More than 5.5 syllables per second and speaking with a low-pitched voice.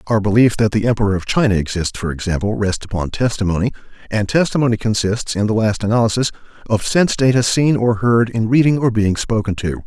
Yes: 6.1 syllables/s; low, 110 Hz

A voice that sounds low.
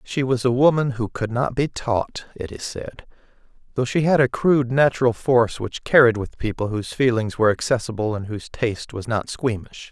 Yes: low, 120 Hz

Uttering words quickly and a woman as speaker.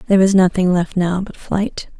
Yes: fast, 210 wpm; female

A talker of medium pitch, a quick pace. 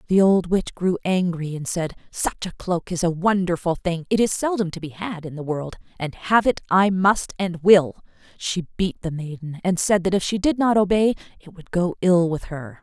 Yes: medium, 180 Hz; fast, 225 wpm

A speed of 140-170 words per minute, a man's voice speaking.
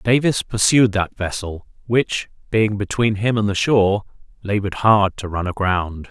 Yes: average, 155 wpm; male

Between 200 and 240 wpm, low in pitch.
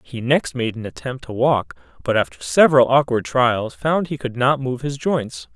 Yes: fast, 205 wpm; low, 125 Hz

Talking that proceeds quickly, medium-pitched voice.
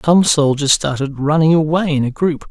No: average, 190 wpm; medium, 150 Hz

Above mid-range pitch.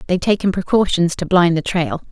No: medium, 180 Hz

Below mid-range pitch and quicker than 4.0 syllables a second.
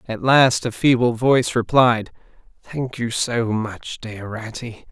No: low, 115 Hz; 3.9 syllables/s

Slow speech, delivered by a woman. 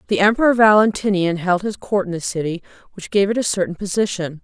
No: fast, 205 wpm; female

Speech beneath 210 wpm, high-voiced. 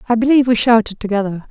Yes: average, 200 wpm; high, 225 Hz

